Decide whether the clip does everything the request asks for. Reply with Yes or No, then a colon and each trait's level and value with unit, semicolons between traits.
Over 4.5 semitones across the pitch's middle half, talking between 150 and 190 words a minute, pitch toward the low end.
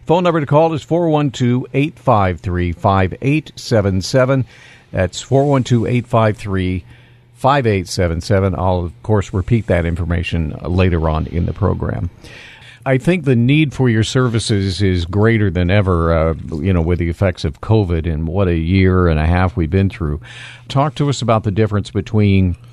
Yes: wide, 5.5 semitones; average, 155 wpm; low, 105 Hz